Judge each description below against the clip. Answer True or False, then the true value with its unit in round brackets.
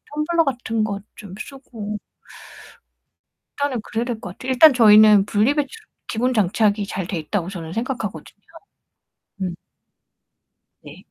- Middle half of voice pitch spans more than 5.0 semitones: False (4.2 semitones)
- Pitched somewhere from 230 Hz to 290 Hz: False (220 Hz)